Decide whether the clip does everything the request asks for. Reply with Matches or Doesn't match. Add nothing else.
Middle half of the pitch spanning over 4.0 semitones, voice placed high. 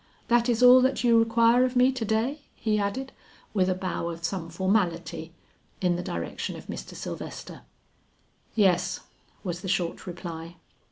Matches